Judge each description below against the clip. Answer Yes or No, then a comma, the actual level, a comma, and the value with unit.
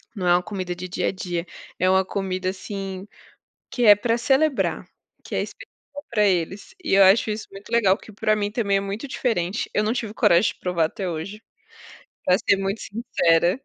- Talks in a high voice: Yes, high, 195 Hz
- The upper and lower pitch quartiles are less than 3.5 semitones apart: Yes, average, 2.8 semitones